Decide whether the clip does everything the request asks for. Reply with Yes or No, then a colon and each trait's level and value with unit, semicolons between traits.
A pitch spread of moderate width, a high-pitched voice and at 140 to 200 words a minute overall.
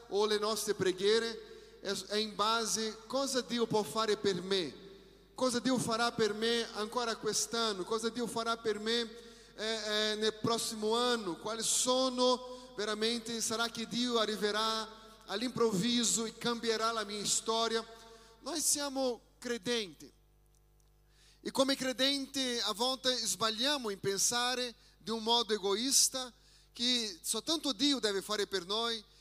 No: narrow, 2.2 semitones; high, 225 Hz; average, 145 wpm